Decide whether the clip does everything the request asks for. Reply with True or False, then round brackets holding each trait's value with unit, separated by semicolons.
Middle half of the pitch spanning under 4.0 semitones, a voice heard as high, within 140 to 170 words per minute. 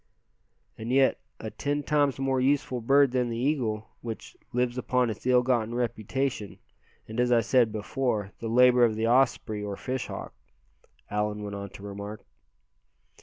False (3.1 semitones; 120 Hz; 165 wpm)